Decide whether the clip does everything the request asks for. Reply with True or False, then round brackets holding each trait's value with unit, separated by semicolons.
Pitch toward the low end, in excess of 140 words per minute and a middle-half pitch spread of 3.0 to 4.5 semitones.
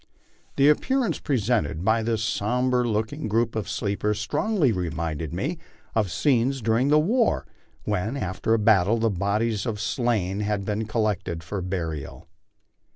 True (110 Hz; 150 wpm; 3.7 semitones)